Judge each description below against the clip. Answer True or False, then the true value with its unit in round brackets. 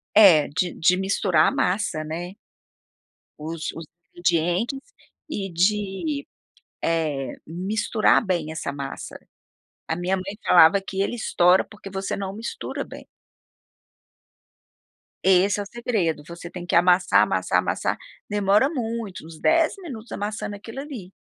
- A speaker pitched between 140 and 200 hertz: True (190 Hz)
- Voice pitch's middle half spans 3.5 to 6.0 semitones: True (3.9 semitones)